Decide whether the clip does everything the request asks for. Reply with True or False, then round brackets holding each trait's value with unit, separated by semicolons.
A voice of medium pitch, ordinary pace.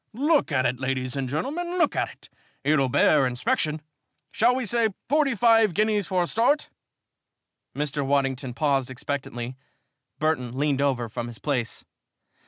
True (145 Hz; 150 wpm)